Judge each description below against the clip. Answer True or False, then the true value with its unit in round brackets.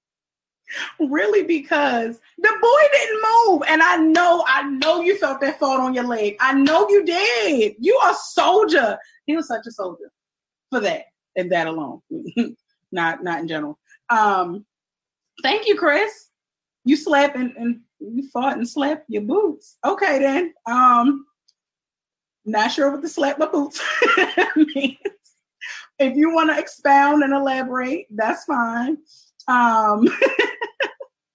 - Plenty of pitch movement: True (6.0 semitones)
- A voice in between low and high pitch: False (290 Hz)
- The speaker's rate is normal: True (145 wpm)